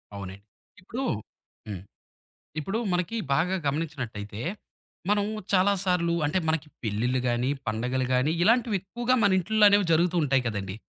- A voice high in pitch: No, medium, 160 Hz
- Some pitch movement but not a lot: No, wide, 8.2 semitones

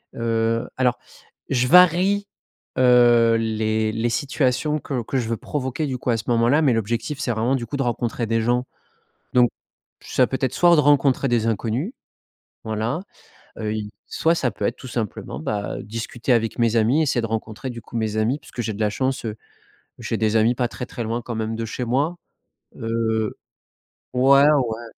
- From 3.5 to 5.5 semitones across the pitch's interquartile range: No, average, 2.9 semitones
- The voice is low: Yes, low, 120 Hz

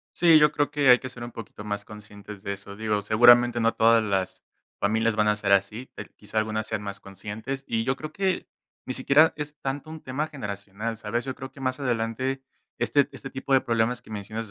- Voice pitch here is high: No, low, 115 Hz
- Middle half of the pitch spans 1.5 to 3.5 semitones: No, average, 4.1 semitones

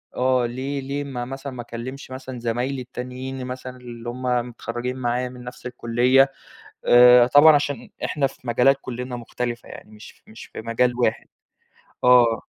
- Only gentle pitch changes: Yes, narrow, 1.5 semitones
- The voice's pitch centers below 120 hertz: No, low, 125 Hz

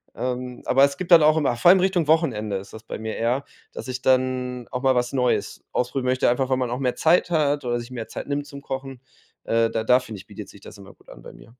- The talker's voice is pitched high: No, low, 125 Hz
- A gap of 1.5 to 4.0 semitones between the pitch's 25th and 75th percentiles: Yes, average, 2.9 semitones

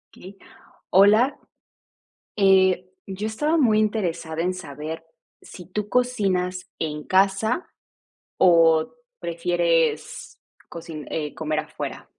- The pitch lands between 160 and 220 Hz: Yes, medium, 185 Hz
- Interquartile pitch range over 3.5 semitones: Yes, average, 4.1 semitones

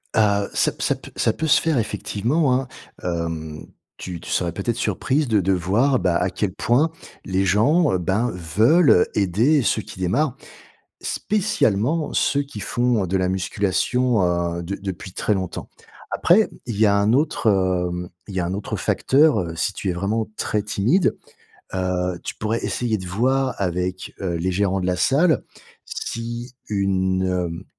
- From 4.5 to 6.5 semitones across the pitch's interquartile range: Yes, average, 5.2 semitones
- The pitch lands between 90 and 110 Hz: Yes, low, 100 Hz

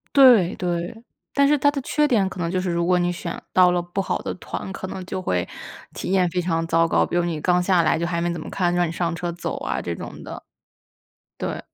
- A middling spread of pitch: No, narrow, 1.8 semitones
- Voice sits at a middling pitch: Yes, medium, 175 Hz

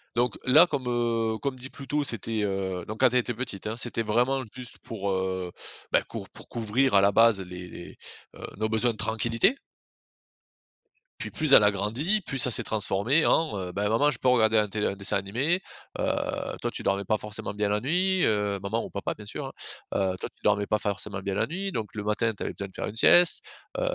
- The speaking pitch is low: Yes, low, 110 Hz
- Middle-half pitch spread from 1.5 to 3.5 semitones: No, average, 4.0 semitones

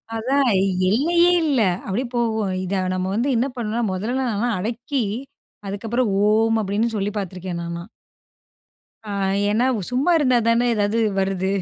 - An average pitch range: Yes, average, 3.8 semitones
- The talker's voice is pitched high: Yes, high, 225 Hz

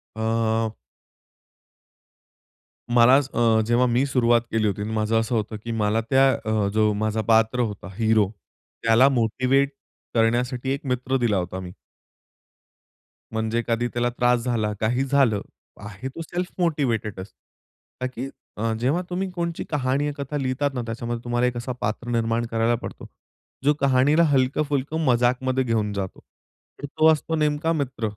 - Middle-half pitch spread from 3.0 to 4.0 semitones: Yes, average, 3.3 semitones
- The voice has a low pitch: Yes, low, 120 Hz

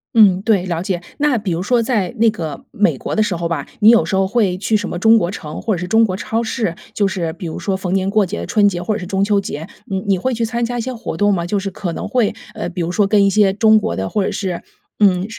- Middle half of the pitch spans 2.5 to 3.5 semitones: Yes, average, 3.2 semitones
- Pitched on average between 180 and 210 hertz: Yes, high, 200 Hz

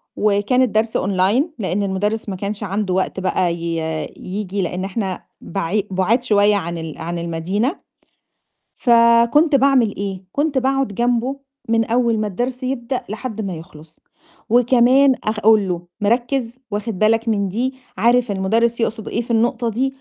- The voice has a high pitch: Yes, high, 215 Hz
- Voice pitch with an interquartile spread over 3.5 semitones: Yes, average, 4.0 semitones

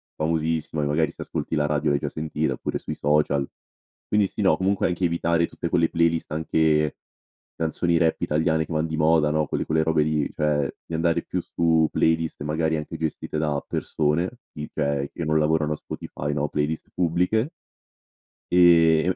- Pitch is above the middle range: No, very low, 80 Hz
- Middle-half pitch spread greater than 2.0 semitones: No, narrow, 1.6 semitones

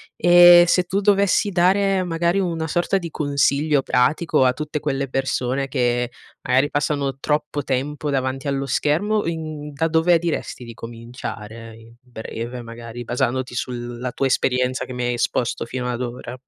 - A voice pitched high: No, low, 135 Hz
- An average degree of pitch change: Yes, average, 4.7 semitones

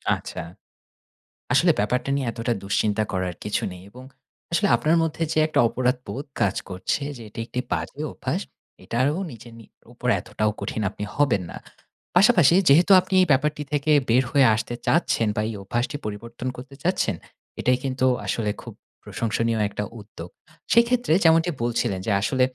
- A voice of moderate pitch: No, low, 125 Hz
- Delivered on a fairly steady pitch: No, average, 5.3 semitones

